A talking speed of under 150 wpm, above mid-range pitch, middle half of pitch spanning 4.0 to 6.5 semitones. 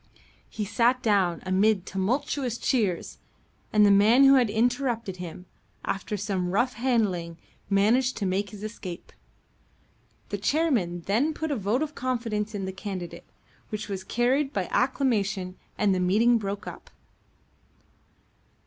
Yes: average, 140 wpm; high, 210 Hz; average, 4.4 semitones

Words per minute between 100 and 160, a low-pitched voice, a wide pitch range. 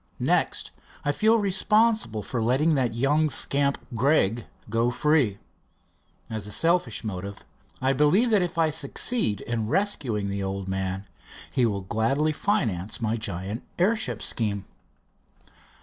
Yes: slow, 135 wpm; low, 120 Hz; wide, 7.3 semitones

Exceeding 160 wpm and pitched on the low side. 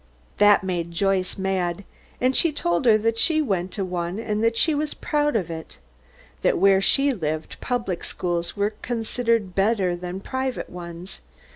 No: average, 170 wpm; high, 195 Hz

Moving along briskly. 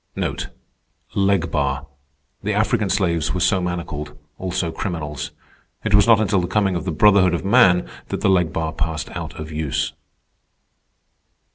No: average, 145 wpm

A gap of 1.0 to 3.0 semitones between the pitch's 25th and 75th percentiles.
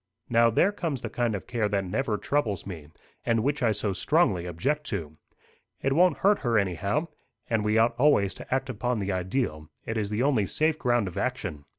No: wide, 5.4 semitones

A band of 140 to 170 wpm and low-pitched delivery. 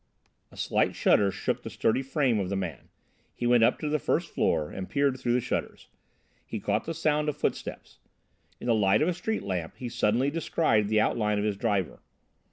No: fast, 205 wpm; low, 115 Hz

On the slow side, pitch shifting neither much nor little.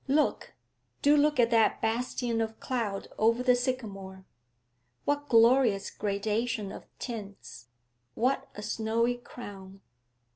Yes: slow, 115 wpm; average, 3.4 semitones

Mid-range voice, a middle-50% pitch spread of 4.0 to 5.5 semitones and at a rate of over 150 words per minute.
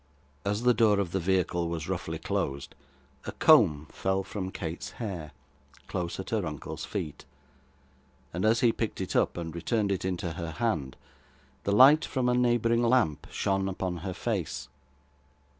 No: very low, 95 Hz; average, 4.9 semitones; average, 160 wpm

